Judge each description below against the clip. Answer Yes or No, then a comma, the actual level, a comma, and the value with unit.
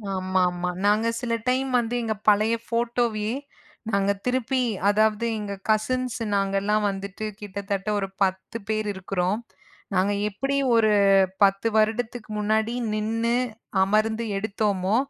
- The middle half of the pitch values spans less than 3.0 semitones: Yes, narrow, 2.6 semitones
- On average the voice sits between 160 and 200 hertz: No, high, 215 Hz